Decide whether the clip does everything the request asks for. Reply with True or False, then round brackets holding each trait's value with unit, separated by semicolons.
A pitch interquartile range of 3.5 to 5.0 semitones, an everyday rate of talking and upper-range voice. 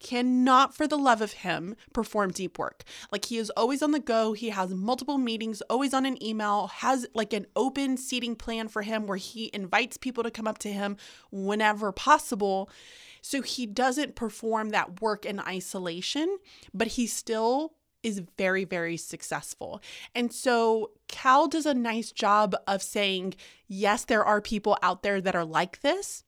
True (3.8 semitones; 175 wpm; 225 Hz)